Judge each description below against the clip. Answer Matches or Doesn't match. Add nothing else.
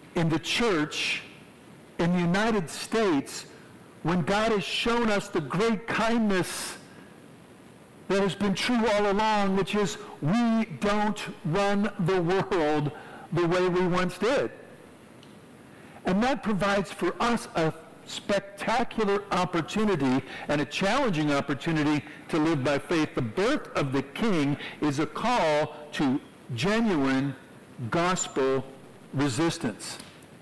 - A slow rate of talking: Matches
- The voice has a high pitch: Doesn't match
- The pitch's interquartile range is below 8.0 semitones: Matches